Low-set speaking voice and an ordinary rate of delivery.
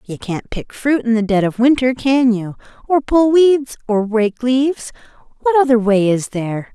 No: high, 240 Hz; average, 195 wpm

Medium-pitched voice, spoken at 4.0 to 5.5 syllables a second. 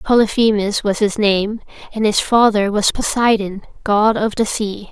No: high, 210 Hz; 4.5 syllables/s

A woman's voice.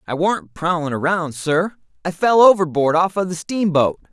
No: male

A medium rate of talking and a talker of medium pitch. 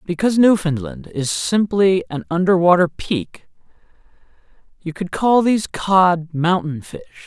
No: slow, 115 wpm; medium, 170 Hz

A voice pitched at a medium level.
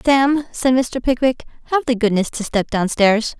No: high, 245 Hz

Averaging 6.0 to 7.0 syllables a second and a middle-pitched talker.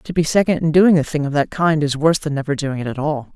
Yes: 6.4 syllables/s; medium, 150 Hz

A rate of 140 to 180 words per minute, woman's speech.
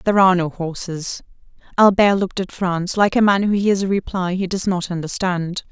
No: average, 200 wpm; female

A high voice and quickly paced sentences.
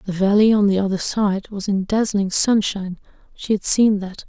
No: high, 200 Hz; average, 180 wpm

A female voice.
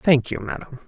No: male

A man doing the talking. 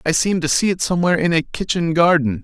Yes: male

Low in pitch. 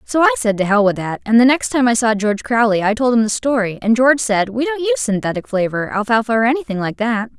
No: high, 235 Hz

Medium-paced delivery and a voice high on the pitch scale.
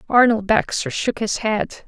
Yes: average, 160 wpm; high, 225 Hz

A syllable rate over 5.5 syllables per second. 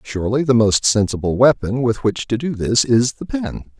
No: 5.0 syllables/s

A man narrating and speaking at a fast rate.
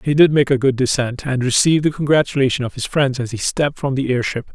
Yes: male; fast, 250 wpm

